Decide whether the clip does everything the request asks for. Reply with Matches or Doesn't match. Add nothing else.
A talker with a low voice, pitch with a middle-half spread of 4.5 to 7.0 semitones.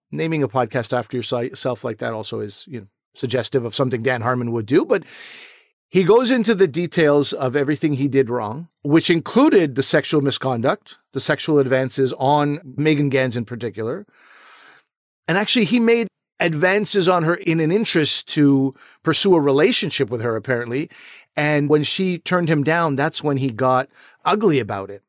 Doesn't match